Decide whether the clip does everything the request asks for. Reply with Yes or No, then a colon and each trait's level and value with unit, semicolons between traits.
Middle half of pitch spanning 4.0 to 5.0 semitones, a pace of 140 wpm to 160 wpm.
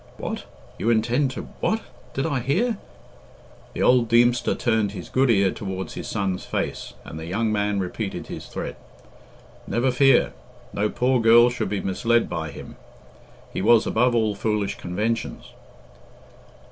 No: average, 3.6 semitones; average, 155 wpm